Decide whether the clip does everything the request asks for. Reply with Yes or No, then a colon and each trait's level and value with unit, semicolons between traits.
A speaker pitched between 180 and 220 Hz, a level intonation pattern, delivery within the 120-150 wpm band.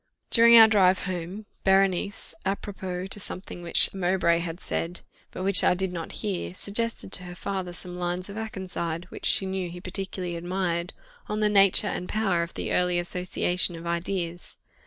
No: medium, 185 Hz; narrow, 1.9 semitones; average, 175 wpm